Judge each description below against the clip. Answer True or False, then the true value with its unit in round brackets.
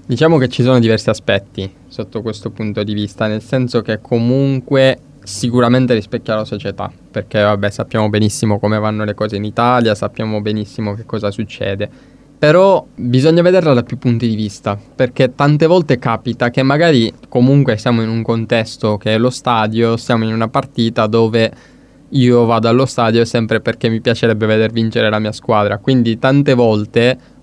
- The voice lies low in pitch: True (115 Hz)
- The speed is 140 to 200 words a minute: True (170 wpm)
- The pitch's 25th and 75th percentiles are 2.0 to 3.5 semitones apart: True (2.8 semitones)